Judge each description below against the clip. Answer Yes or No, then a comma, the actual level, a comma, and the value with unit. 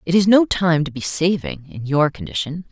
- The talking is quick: Yes, fast, 220 wpm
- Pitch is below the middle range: No, medium, 155 Hz